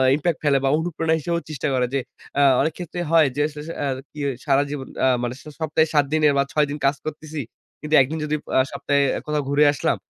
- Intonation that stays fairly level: Yes, narrow, 1.9 semitones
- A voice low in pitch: No, medium, 150 Hz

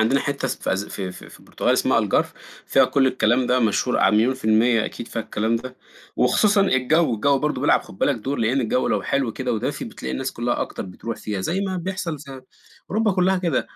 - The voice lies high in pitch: No, low, 130 Hz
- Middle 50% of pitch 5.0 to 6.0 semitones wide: Yes, wide, 5.6 semitones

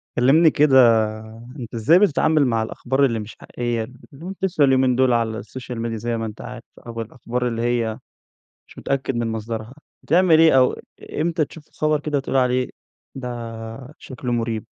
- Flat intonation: No, average, 3.6 semitones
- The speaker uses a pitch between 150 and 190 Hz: No, low, 125 Hz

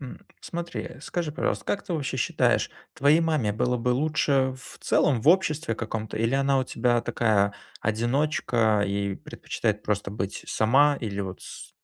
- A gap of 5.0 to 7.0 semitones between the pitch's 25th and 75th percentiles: Yes, average, 5.3 semitones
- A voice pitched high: No, low, 125 Hz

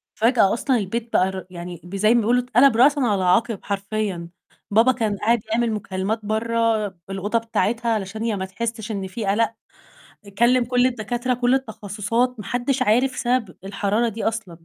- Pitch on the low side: No, high, 225 Hz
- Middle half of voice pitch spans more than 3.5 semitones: No, average, 3.2 semitones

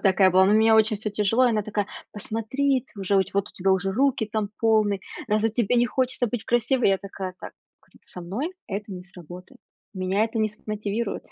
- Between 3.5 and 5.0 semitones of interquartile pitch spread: No, average, 2.8 semitones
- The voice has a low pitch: No, high, 210 Hz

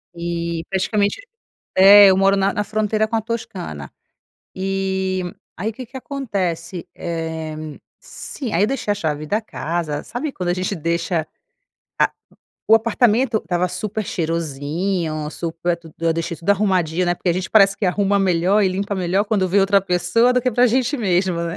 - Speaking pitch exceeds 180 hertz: Yes, high, 190 Hz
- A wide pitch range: No, average, 3.8 semitones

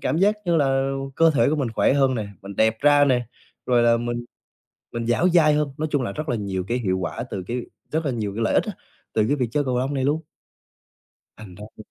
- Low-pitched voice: Yes, low, 125 Hz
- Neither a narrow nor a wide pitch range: Yes, average, 4.5 semitones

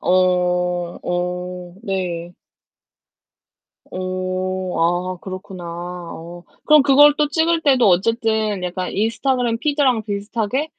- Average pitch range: Yes, average, 4.5 semitones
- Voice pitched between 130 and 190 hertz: Yes, medium, 185 Hz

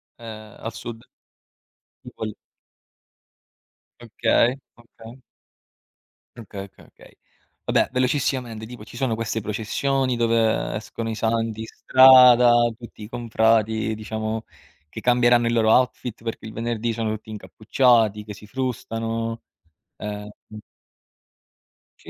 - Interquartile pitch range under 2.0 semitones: Yes, narrow, 1.6 semitones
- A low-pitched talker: Yes, low, 115 Hz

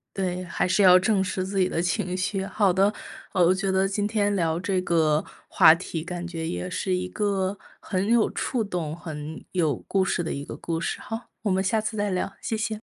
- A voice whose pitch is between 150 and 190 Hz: Yes, medium, 185 Hz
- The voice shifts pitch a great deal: No, average, 2.7 semitones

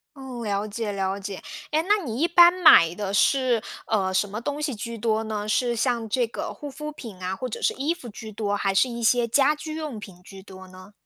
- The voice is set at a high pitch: Yes, high, 225 Hz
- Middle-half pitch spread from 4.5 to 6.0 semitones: Yes, average, 5.0 semitones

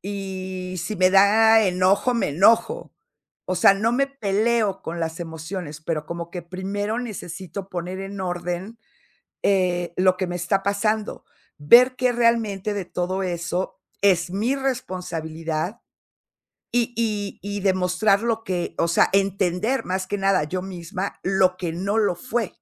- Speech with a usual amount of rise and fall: Yes, average, 3.1 semitones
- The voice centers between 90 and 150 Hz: No, high, 190 Hz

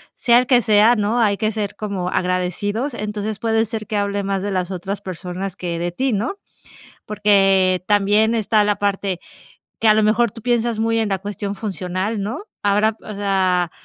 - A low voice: No, high, 205 Hz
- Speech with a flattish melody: Yes, narrow, 2.3 semitones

